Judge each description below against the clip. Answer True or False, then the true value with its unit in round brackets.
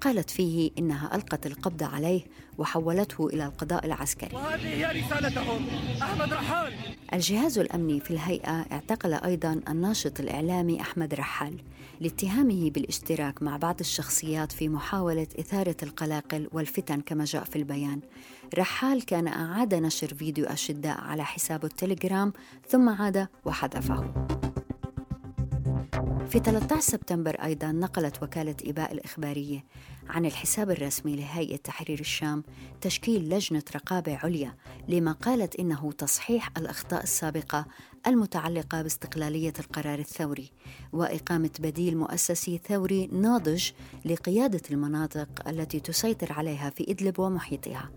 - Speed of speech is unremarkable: True (110 wpm)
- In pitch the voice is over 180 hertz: False (160 Hz)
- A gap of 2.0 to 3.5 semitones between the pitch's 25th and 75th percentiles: True (3.2 semitones)